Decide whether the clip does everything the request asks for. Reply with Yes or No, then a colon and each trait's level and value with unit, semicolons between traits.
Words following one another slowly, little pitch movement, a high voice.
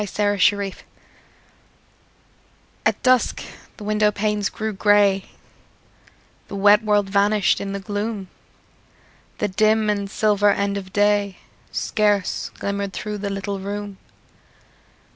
Yes: slow, 110 wpm; narrow, 0.9 semitones; high, 205 Hz